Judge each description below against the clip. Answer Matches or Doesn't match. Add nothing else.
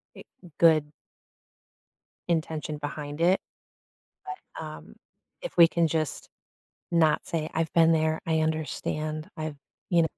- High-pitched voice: Doesn't match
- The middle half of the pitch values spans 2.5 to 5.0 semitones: Doesn't match